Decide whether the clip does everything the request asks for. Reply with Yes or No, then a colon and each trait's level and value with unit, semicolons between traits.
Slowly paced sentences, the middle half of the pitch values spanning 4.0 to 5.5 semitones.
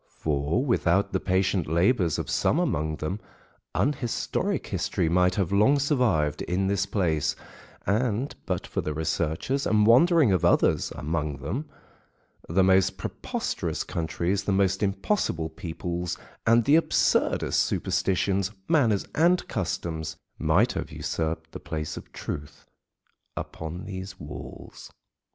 Yes: slow, 130 wpm; average, 5.2 semitones